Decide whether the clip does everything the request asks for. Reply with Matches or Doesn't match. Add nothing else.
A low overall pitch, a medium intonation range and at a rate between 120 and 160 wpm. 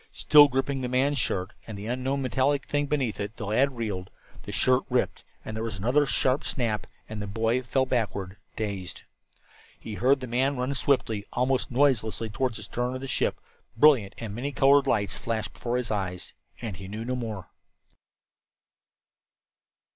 Doesn't match